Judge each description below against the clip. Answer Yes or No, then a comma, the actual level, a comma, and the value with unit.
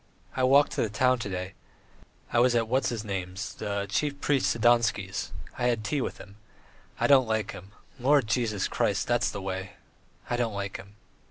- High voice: No, low, 110 Hz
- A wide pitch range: No, average, 4.0 semitones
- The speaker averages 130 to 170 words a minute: No, average, 190 wpm